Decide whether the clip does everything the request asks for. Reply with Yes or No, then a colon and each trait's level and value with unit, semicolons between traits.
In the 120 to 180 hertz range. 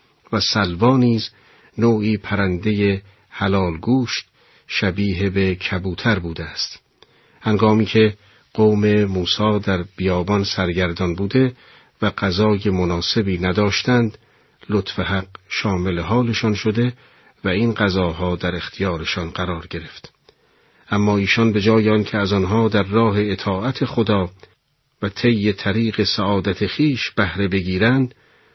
No: low, 100 Hz